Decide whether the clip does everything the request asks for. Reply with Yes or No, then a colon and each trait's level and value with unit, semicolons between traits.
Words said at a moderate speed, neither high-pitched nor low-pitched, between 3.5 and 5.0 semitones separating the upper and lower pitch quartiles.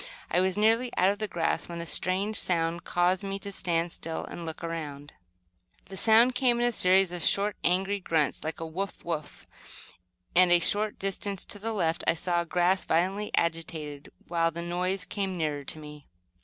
No: average, 195 wpm; medium, 180 Hz; average, 3.0 semitones